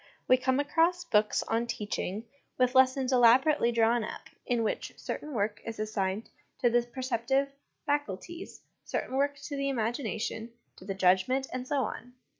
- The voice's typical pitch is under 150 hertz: No, high, 245 Hz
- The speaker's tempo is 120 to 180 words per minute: Yes, average, 160 wpm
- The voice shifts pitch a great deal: No, average, 3.5 semitones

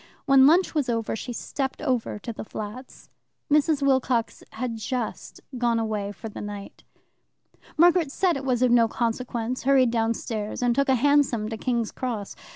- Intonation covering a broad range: No, average, 3.3 semitones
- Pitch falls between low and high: No, high, 245 Hz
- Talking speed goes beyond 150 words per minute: Yes, average, 170 wpm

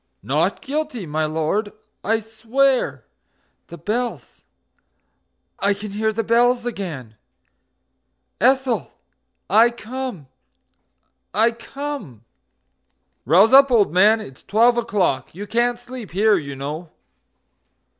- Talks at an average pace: No, slow, 105 wpm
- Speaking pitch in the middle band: No, high, 220 Hz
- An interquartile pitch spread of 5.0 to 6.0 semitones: Yes, wide, 5.5 semitones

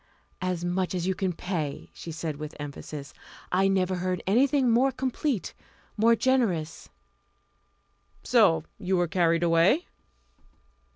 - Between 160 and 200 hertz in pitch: Yes, medium, 185 Hz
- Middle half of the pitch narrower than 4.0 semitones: No, average, 5.2 semitones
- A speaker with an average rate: No, slow, 125 wpm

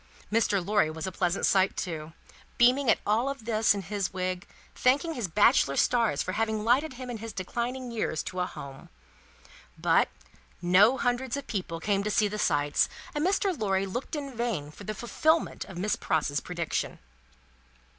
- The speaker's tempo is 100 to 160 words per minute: No, average, 180 wpm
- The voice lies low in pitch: No, high, 210 Hz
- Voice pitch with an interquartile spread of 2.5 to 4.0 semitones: No, average, 5.1 semitones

